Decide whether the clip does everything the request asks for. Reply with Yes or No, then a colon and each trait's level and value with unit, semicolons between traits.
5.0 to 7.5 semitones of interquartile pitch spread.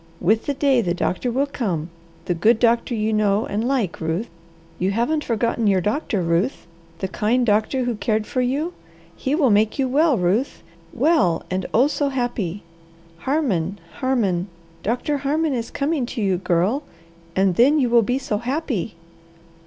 Yes: wide, 5.4 semitones